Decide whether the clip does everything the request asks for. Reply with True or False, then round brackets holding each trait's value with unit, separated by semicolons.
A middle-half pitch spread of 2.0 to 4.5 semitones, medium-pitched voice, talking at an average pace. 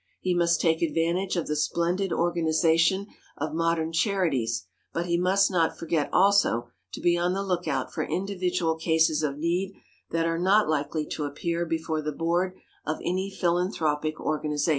True (2.4 semitones; 170 Hz; 160 wpm)